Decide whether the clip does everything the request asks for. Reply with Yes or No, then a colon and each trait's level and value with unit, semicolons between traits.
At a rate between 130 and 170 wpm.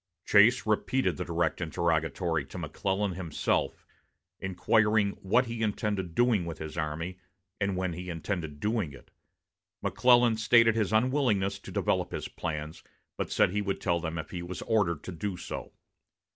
Yes: average, 160 wpm